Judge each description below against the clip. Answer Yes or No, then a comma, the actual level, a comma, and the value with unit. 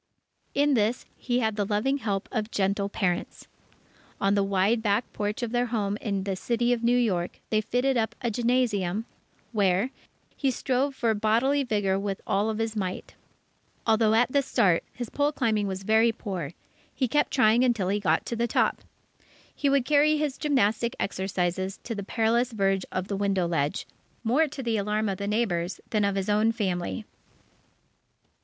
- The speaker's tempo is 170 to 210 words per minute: Yes, average, 175 wpm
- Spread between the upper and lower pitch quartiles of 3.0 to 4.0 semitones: Yes, average, 3.6 semitones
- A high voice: Yes, high, 215 Hz